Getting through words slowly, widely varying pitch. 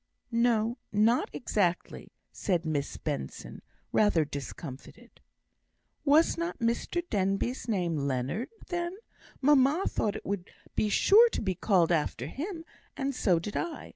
Yes: slow, 130 wpm; wide, 8.3 semitones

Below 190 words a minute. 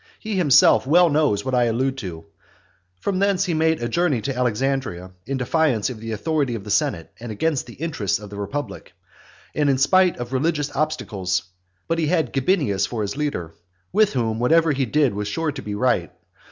No: average, 195 wpm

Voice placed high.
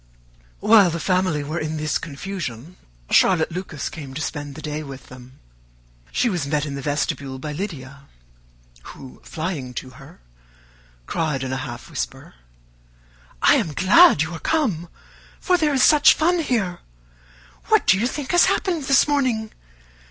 No: medium, 160 Hz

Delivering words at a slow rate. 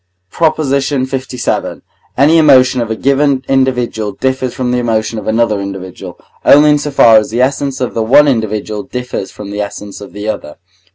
No: average, 180 wpm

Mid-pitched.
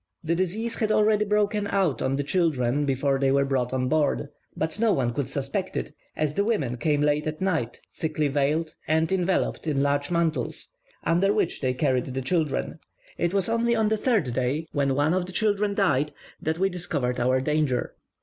Yes: medium, 155 Hz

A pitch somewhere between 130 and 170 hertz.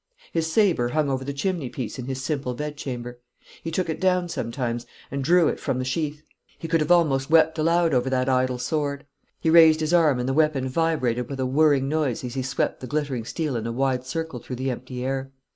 Yes: medium, 140 Hz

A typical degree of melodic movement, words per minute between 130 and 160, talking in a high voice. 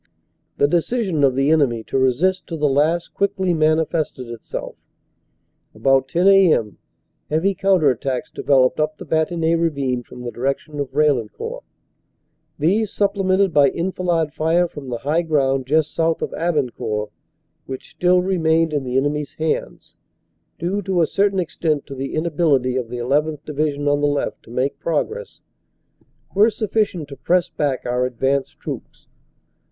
No: average, 4.4 semitones; average, 155 wpm; medium, 155 Hz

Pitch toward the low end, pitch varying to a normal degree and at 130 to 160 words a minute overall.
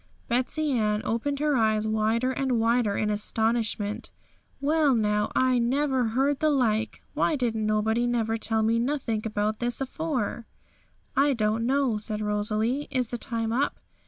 No: high, 230 Hz; average, 3.4 semitones; average, 155 wpm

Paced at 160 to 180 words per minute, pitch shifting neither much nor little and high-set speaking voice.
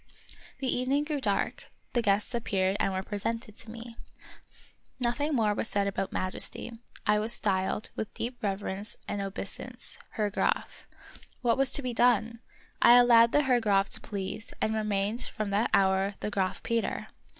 Yes: average, 165 wpm; average, 3.2 semitones; high, 215 Hz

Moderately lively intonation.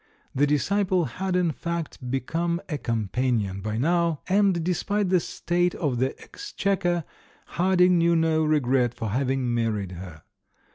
No: wide, 6.3 semitones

